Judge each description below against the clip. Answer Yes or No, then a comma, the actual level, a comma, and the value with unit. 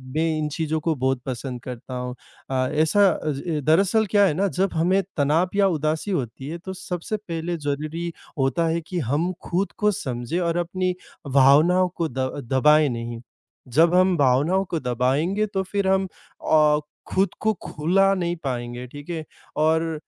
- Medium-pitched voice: Yes, medium, 160 Hz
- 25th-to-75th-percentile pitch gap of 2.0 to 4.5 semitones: No, average, 5.0 semitones